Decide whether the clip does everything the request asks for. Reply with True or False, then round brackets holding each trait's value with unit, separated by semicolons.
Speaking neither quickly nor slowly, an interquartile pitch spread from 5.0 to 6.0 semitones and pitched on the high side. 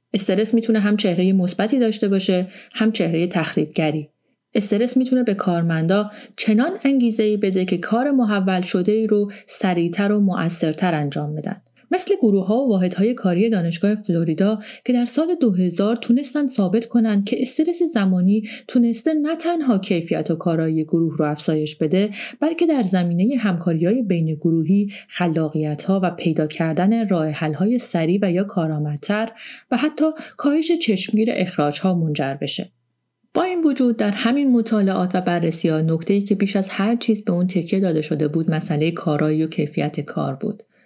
False (165 wpm; 5.4 semitones; 195 Hz)